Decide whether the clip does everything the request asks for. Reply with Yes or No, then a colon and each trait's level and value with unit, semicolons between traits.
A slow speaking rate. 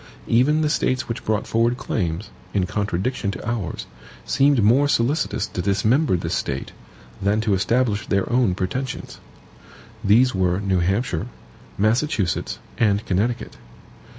Yes: slow, 130 wpm